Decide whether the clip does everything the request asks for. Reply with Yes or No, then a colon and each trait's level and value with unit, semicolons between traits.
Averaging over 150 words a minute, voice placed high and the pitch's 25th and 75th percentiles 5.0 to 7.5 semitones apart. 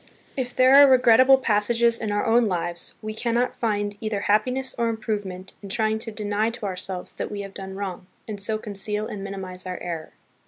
No: average, 200 wpm; high, 210 Hz; average, 2.8 semitones